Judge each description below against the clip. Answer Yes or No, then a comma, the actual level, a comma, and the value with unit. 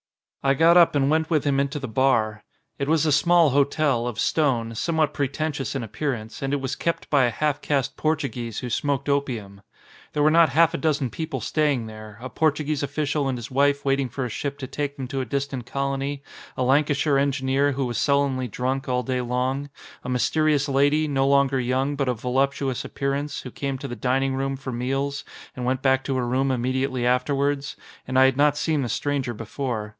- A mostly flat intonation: Yes, narrow, 2.1 semitones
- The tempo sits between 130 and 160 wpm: No, fast, 205 wpm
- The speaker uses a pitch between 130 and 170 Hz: Yes, low, 135 Hz